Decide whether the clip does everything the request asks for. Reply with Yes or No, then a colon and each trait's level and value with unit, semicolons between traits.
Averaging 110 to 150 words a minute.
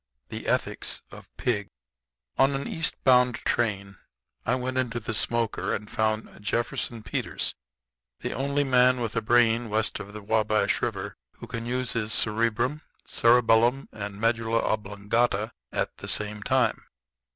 Yes: average, 145 wpm